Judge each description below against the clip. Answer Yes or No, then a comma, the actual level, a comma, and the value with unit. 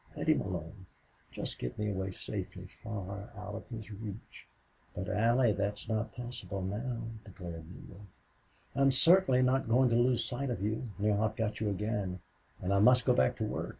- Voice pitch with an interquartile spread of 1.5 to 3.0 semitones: No, average, 3.4 semitones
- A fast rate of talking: No, average, 185 wpm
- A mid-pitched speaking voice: No, low, 105 Hz